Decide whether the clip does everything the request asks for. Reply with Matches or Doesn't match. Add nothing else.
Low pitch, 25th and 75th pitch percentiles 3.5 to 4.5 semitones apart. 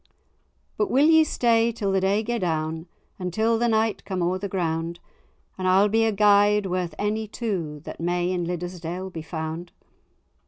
Doesn't match